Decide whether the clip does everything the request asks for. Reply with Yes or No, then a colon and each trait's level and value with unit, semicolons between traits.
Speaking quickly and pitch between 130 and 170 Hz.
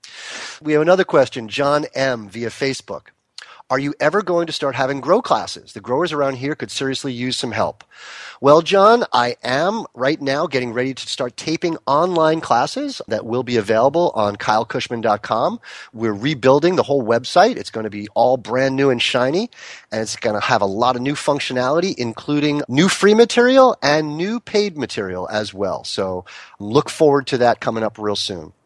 No: average, 185 wpm; low, 135 Hz